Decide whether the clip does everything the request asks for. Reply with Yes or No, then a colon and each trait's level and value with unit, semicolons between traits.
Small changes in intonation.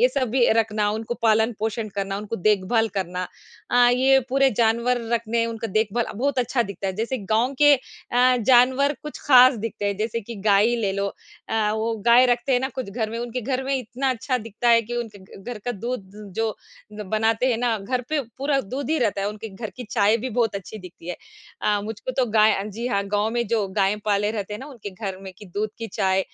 No: average, 3.1 semitones